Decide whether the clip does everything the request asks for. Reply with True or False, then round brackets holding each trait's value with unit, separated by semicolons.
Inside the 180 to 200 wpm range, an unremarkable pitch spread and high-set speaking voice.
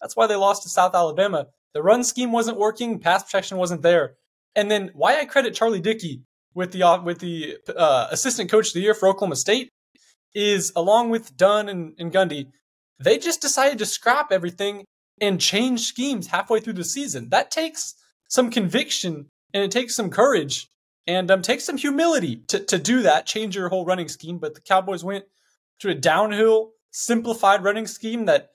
True (190 wpm; 4.2 semitones; 205 Hz)